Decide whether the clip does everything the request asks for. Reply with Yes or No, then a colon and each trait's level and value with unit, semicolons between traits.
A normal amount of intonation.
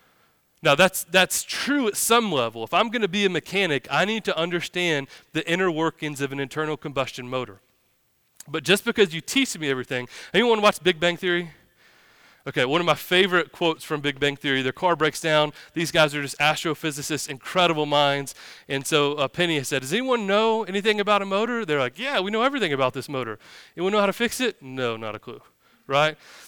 No: wide, 5.7 semitones